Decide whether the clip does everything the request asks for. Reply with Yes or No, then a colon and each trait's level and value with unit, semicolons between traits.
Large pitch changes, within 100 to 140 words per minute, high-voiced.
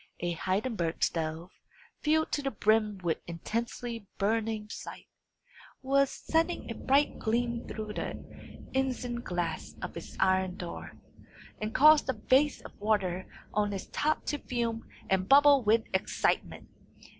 Yes: wide, 5.7 semitones; slow, 135 wpm; high, 225 Hz